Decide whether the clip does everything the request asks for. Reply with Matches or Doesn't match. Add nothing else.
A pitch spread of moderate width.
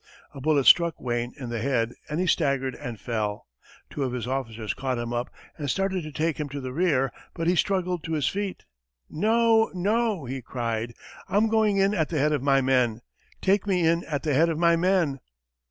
Doesn't match